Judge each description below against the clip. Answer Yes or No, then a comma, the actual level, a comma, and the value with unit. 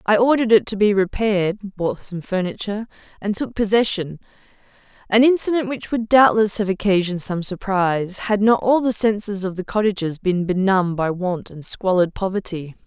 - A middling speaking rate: Yes, average, 170 wpm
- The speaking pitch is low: No, high, 200 Hz